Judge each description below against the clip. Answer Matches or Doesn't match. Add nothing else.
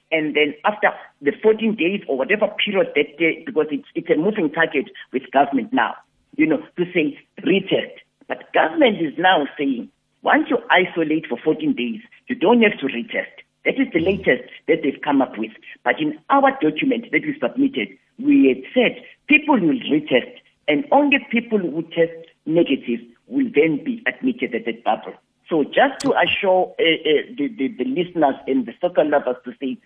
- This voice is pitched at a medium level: Matches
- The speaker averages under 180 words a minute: Doesn't match